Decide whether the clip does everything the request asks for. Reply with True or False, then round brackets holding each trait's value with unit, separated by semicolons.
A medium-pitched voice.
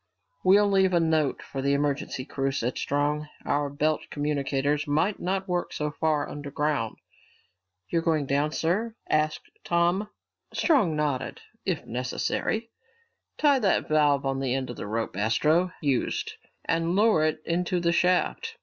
True (155 Hz)